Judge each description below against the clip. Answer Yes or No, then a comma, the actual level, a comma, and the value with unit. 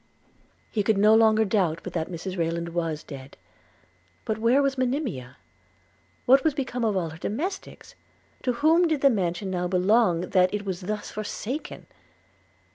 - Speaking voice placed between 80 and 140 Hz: No, high, 205 Hz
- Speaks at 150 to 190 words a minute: Yes, average, 165 wpm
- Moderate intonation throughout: No, wide, 6.2 semitones